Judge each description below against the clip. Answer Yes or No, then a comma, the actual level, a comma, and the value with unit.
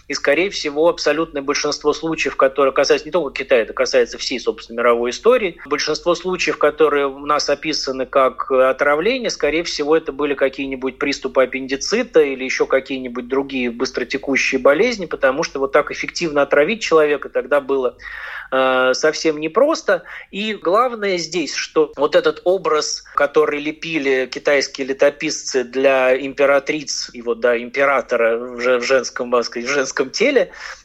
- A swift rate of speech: No, average, 140 wpm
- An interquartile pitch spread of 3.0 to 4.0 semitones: Yes, average, 3.4 semitones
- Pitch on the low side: No, medium, 145 Hz